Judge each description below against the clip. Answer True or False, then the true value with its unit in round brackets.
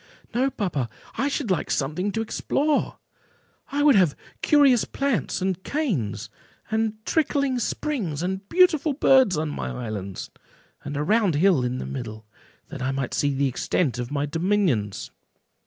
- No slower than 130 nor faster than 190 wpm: True (155 wpm)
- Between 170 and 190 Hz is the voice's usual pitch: True (185 Hz)